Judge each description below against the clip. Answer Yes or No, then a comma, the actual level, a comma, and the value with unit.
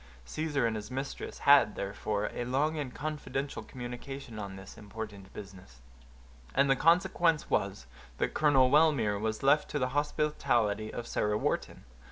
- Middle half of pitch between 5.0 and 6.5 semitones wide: Yes, wide, 5.6 semitones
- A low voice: Yes, low, 125 Hz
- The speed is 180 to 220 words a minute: No, average, 150 wpm